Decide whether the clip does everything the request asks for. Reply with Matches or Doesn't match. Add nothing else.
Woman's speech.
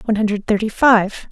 Matches